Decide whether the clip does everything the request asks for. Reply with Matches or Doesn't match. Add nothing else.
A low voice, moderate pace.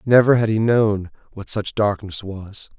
Matches